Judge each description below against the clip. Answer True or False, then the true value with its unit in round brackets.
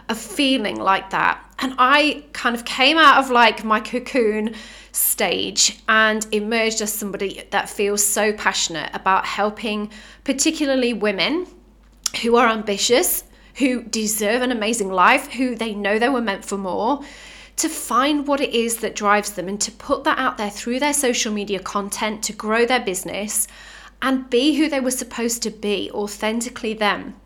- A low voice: False (225 Hz)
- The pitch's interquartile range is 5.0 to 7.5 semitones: False (3.7 semitones)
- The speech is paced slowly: False (165 wpm)